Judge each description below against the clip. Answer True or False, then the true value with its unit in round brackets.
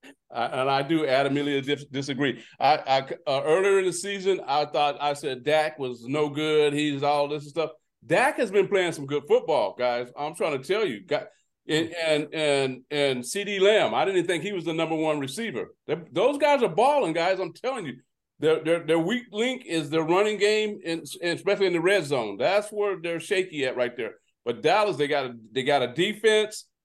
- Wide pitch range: True (5.7 semitones)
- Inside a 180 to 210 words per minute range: True (205 wpm)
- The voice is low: False (160 Hz)